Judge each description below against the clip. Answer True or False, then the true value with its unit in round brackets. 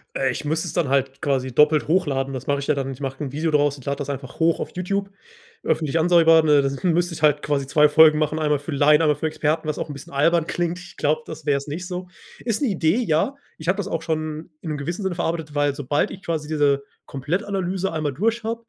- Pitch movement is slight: False (3.2 semitones)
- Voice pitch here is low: False (155 Hz)